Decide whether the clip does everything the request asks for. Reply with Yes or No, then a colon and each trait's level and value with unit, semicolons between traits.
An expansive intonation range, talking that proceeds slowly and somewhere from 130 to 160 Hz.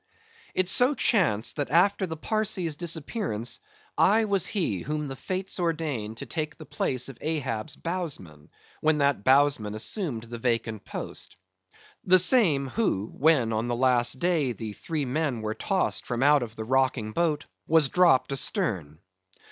No: wide, 6.5 semitones; average, 155 wpm; medium, 140 Hz